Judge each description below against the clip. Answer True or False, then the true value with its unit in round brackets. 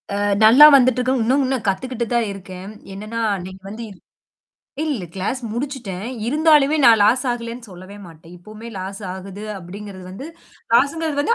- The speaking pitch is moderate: False (225 Hz)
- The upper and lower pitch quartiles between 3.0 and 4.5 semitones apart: False (5.2 semitones)